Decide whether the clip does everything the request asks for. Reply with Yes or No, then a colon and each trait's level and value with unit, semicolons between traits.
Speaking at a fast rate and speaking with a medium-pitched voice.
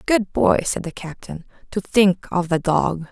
No: average, 195 wpm; medium, 180 Hz